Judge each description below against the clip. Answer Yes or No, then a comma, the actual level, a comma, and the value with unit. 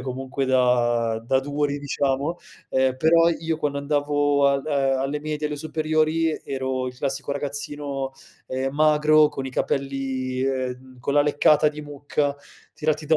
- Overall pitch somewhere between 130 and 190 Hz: Yes, medium, 140 Hz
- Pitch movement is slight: Yes, narrow, 2.1 semitones